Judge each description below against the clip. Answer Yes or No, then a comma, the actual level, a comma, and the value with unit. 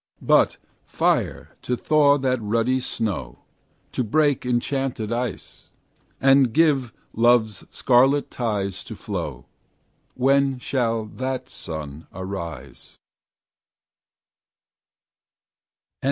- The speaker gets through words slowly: Yes, slow, 85 wpm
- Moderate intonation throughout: Yes, average, 4.7 semitones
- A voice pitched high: No, low, 120 Hz